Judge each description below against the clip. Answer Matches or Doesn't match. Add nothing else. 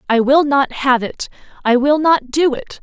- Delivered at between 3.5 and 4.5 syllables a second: Matches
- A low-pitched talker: Doesn't match